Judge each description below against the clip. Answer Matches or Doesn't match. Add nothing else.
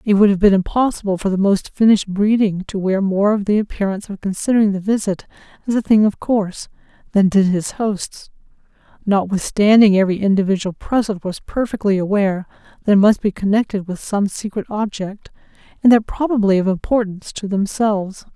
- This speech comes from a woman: Matches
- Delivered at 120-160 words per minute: Doesn't match